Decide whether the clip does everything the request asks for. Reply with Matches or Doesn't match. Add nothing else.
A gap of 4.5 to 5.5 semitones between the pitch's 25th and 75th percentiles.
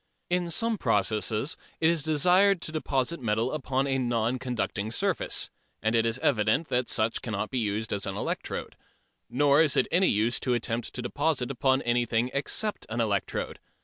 Matches